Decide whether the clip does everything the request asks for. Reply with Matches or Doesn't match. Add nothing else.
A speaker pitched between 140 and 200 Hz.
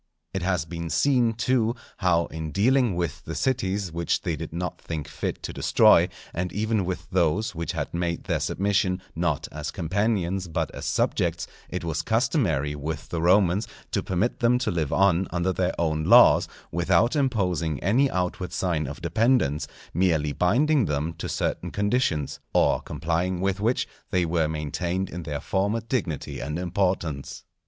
Doesn't match